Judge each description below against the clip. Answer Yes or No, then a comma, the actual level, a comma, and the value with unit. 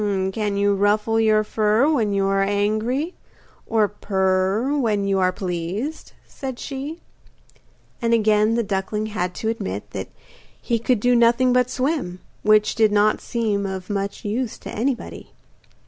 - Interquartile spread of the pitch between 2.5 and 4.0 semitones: Yes, average, 3.0 semitones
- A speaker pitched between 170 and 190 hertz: No, high, 215 Hz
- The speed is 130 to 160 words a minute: Yes, average, 150 wpm